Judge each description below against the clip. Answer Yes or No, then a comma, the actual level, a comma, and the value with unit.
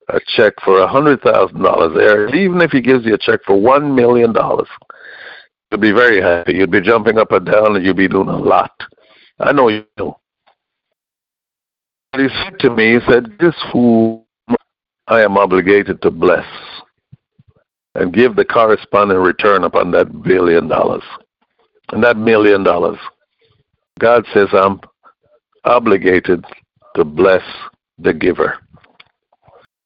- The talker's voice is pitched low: Yes, low, 115 Hz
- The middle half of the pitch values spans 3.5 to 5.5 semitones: Yes, average, 4.6 semitones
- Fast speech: No, average, 145 wpm